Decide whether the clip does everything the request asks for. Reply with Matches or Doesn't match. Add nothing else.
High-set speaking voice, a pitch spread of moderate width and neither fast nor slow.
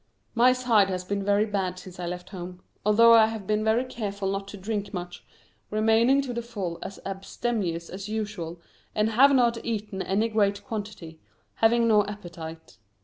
Matches